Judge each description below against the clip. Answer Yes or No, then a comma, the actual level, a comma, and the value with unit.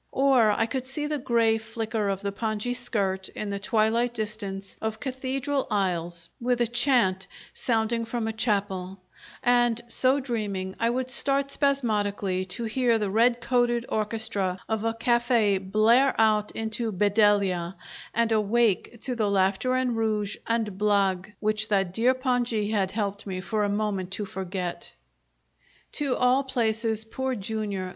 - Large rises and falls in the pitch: No, average, 3.2 semitones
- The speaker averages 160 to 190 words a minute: No, average, 150 wpm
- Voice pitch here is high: Yes, high, 220 Hz